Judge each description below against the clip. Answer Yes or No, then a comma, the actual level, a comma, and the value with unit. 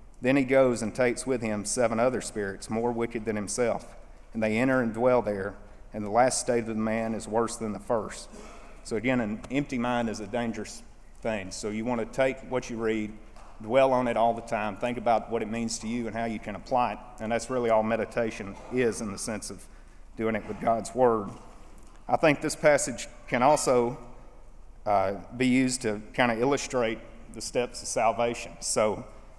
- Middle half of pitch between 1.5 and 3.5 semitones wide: Yes, narrow, 2.4 semitones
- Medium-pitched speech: No, low, 115 Hz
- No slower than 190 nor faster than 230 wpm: Yes, fast, 205 wpm